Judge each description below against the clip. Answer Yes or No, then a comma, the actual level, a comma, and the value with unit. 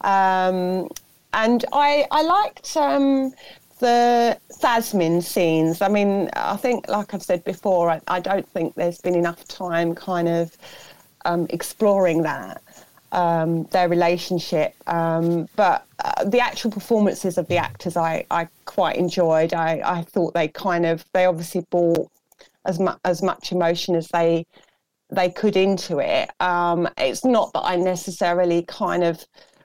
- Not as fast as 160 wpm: Yes, average, 150 wpm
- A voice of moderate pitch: Yes, medium, 180 Hz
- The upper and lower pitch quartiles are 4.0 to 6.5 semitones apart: No, average, 2.8 semitones